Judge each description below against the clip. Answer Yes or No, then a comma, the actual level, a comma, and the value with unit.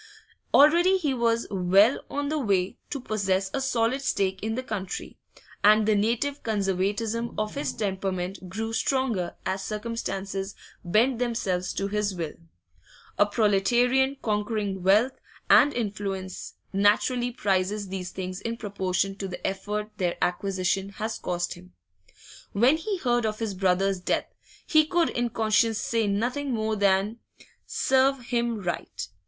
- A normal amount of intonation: Yes, average, 3.7 semitones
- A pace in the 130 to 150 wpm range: Yes, average, 140 wpm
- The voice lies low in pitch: No, high, 210 Hz